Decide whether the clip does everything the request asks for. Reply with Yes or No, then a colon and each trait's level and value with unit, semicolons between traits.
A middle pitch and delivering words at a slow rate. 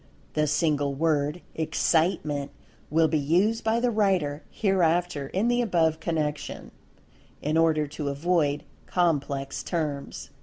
Yes: medium, 160 Hz; slow, 120 wpm